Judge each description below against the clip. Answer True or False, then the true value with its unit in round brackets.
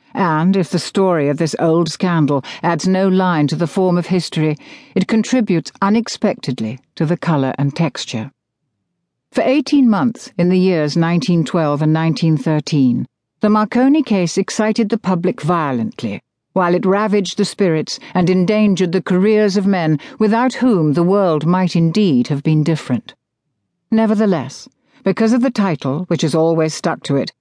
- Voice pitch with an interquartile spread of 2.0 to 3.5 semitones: False (4.5 semitones)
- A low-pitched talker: False (180 Hz)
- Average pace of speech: True (155 wpm)